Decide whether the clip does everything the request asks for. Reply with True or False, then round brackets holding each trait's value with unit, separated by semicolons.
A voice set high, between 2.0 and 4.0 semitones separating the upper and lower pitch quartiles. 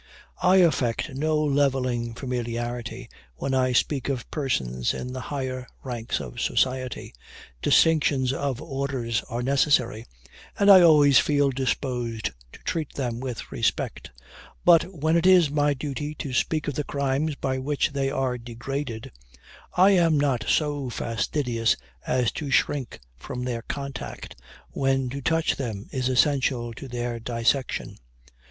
False (135 Hz; 3.2 semitones)